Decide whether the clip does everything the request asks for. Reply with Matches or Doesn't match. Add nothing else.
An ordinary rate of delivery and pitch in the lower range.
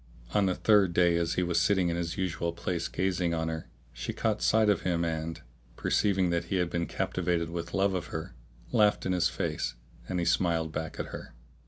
Doesn't match